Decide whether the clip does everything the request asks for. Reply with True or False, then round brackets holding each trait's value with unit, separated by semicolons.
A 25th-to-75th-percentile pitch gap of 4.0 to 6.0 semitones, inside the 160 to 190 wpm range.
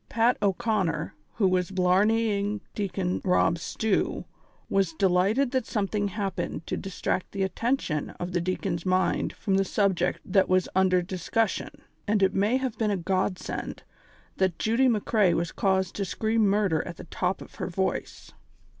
False (2.6 semitones; 170 wpm)